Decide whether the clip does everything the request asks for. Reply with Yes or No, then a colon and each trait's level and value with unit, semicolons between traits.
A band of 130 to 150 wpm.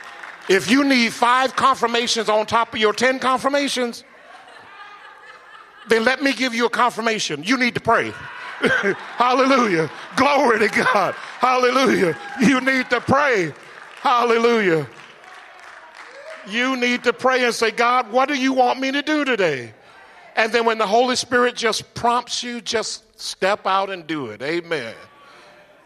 Yes: average, 145 wpm